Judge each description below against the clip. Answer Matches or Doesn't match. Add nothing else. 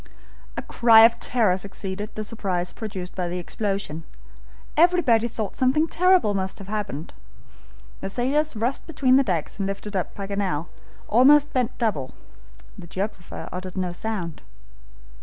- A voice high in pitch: Matches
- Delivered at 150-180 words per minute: Doesn't match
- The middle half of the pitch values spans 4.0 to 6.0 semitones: Matches